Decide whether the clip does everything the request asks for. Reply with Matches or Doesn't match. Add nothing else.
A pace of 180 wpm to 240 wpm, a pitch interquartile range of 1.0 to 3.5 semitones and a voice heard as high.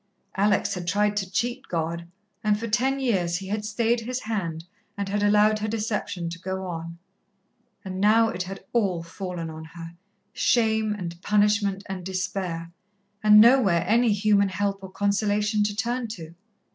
Doesn't match